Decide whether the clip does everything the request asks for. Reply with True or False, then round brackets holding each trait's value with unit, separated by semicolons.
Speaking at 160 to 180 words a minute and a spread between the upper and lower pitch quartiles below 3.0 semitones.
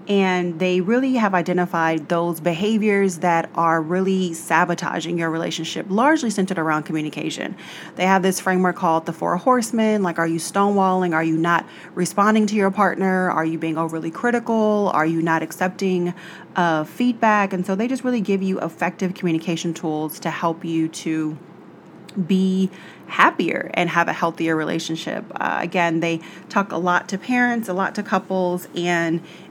True (165 wpm; 2.6 semitones)